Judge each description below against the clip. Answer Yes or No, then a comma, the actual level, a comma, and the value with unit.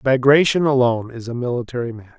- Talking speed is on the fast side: No, average, 165 wpm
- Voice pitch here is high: No, low, 125 Hz